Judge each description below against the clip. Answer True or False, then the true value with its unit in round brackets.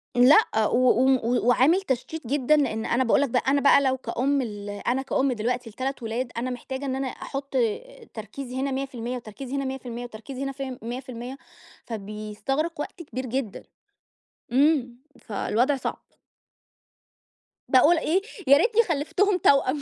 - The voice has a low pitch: False (260 Hz)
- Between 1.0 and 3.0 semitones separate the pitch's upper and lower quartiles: True (2.6 semitones)